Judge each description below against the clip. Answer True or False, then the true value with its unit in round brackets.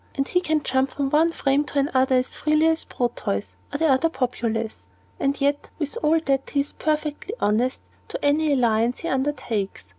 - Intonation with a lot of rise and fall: False (3.3 semitones)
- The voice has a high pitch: True (275 Hz)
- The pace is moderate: True (180 wpm)